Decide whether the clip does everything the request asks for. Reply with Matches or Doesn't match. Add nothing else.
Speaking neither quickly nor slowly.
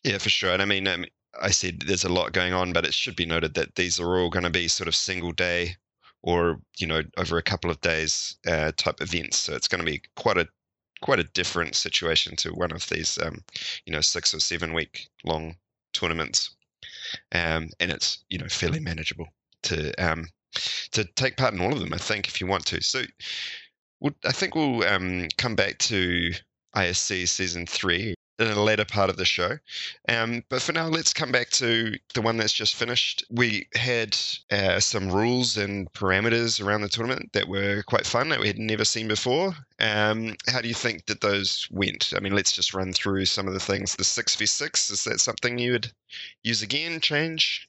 Doesn't match